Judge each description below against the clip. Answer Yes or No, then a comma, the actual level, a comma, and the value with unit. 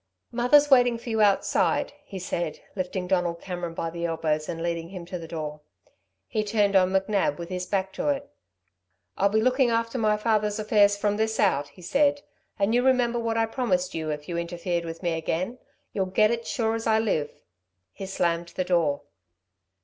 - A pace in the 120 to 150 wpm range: No, average, 195 wpm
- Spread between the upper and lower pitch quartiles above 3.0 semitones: Yes, average, 4.8 semitones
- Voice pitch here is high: Yes, high, 195 Hz